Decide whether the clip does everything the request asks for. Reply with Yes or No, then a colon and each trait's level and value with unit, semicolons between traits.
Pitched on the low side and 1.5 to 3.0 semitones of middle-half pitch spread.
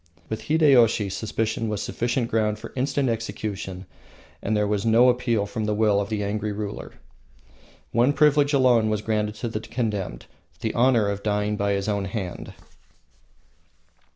Yes: low, 110 Hz; narrow, 2.5 semitones